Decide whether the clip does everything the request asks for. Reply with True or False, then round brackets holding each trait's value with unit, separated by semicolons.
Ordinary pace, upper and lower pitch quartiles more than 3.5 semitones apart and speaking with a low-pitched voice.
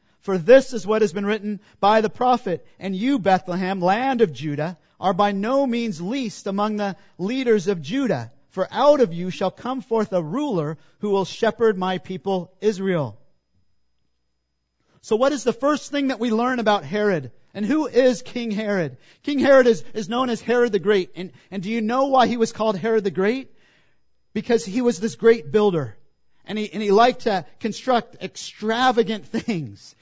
False (185 wpm; 4.4 semitones; 210 Hz)